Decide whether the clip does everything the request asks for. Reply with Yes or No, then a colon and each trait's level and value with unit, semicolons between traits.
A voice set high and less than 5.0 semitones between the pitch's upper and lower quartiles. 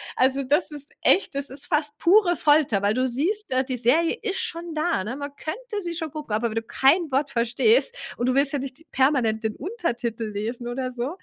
No: very high, 275 Hz; average, 5.3 semitones